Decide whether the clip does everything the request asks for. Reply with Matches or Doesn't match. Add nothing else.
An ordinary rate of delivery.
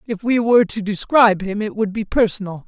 Doesn't match